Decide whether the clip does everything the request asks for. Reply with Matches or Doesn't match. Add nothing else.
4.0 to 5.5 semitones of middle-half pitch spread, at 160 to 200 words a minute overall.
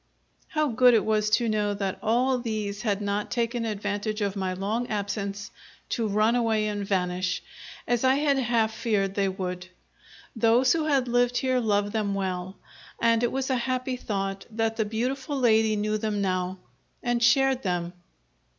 Doesn't match